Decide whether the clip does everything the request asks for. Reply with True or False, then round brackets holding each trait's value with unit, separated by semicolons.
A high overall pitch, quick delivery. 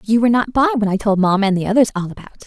True (220 Hz; 340 wpm)